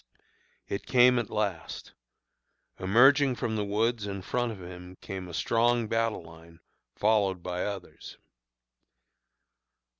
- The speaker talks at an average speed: No, slow, 120 wpm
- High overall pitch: No, low, 105 Hz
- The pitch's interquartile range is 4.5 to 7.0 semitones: No, average, 4.1 semitones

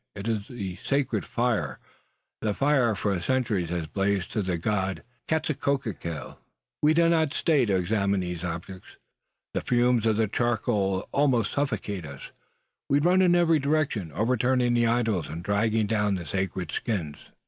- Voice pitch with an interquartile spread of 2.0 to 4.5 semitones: No, wide, 5.5 semitones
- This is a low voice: Yes, low, 110 Hz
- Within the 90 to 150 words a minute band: No, average, 160 wpm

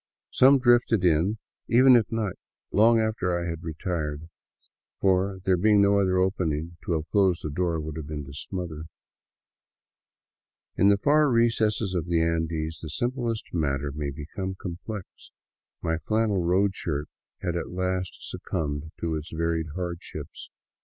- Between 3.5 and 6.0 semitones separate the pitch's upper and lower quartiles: Yes, average, 4.0 semitones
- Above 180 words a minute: No, average, 150 wpm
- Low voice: Yes, very low, 90 Hz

